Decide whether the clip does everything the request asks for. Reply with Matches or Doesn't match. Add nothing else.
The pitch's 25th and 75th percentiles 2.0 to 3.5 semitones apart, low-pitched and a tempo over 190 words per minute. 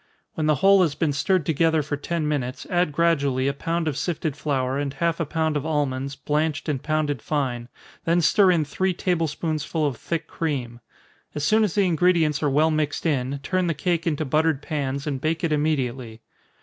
Doesn't match